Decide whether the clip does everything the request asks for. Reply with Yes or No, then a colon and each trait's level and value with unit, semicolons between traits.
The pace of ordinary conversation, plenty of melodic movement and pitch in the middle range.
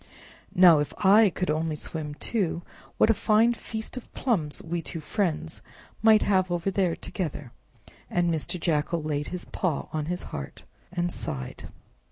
No: average, 160 wpm; average, 4.0 semitones; medium, 175 Hz